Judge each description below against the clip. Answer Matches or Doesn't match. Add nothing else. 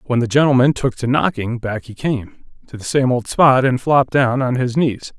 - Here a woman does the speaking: Doesn't match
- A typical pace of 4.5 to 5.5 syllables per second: Matches